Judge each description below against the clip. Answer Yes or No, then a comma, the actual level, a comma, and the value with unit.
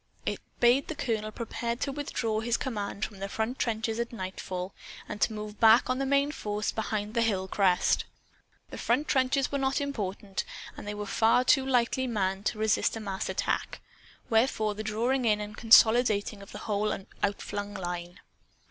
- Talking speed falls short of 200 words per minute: Yes, average, 180 wpm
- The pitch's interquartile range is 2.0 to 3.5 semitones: Yes, average, 3.1 semitones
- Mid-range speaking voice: No, high, 220 Hz